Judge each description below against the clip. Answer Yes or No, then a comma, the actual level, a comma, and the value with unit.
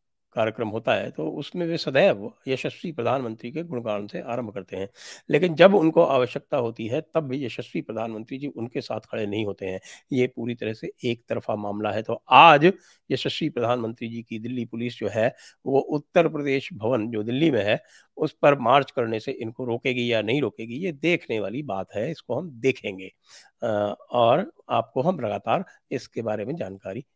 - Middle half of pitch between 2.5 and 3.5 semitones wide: No, average, 4.3 semitones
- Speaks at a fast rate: Yes, fast, 210 wpm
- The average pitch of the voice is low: Yes, low, 120 Hz